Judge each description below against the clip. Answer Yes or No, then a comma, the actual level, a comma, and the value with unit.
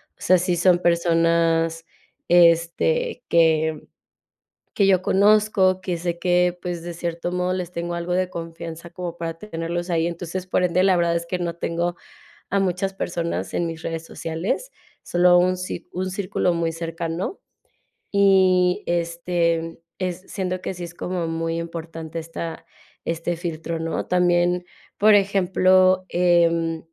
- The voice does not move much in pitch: Yes, narrow, 1.6 semitones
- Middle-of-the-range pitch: Yes, medium, 175 Hz